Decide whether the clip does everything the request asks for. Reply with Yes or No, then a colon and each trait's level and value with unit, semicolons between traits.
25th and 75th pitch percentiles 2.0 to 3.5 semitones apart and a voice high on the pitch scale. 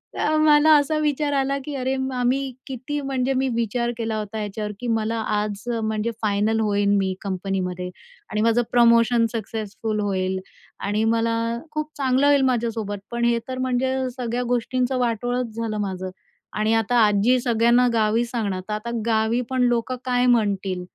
Yes: average, 3.2 semitones; high, 230 Hz